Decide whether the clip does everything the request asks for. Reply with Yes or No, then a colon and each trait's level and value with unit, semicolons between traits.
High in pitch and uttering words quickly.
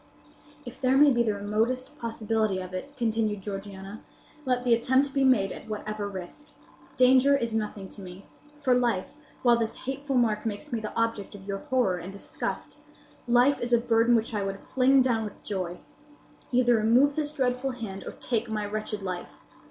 No: high, 230 Hz; average, 175 wpm